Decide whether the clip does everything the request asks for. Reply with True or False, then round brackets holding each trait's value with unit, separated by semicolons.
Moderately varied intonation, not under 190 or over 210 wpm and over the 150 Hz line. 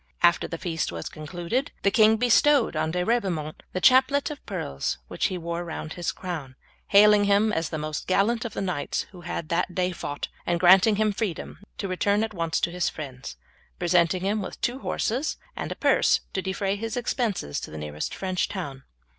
True (4.4 semitones; 195 wpm; 185 Hz)